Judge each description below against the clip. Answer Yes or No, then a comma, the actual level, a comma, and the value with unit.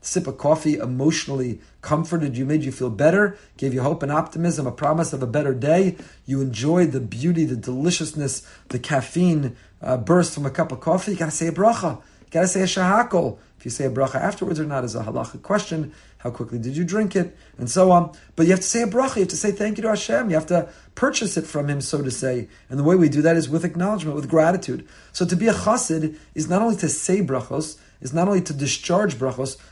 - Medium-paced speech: No, fast, 240 wpm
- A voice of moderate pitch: Yes, medium, 155 Hz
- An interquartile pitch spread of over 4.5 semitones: Yes, average, 5.1 semitones